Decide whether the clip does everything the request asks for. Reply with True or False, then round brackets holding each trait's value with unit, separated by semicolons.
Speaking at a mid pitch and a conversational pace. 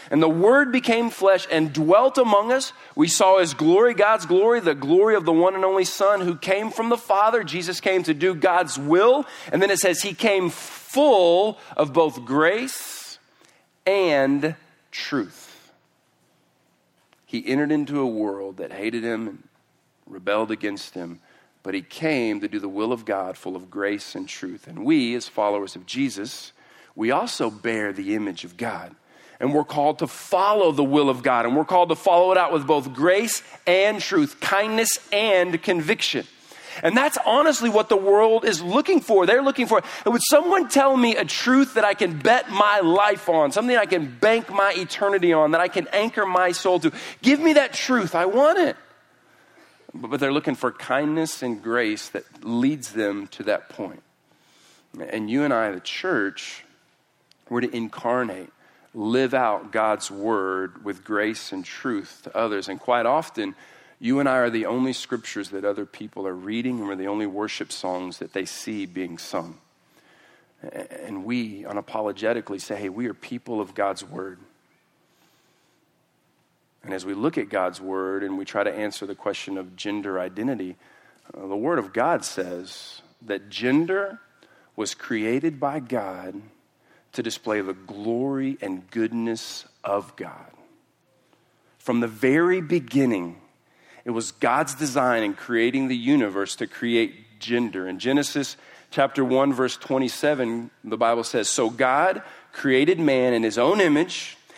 True (150 Hz; 170 wpm)